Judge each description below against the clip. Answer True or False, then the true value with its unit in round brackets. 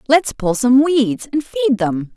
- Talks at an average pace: True (195 wpm)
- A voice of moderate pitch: False (255 Hz)